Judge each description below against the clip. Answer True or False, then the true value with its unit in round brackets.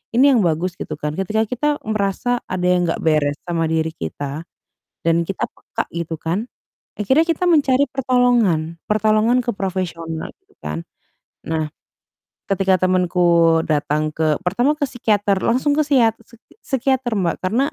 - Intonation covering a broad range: True (6.8 semitones)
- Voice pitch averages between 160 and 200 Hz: True (190 Hz)